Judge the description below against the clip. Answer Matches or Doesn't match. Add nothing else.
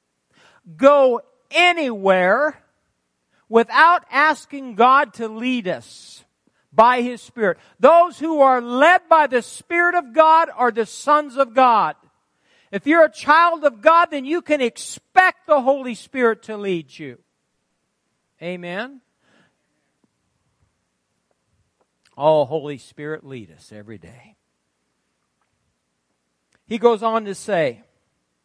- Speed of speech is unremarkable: Doesn't match